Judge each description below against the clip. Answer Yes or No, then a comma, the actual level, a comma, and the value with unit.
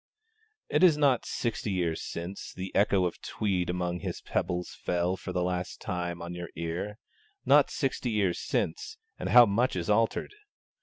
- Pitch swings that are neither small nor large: Yes, average, 4.7 semitones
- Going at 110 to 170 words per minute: Yes, average, 165 wpm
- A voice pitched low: Yes, very low, 95 Hz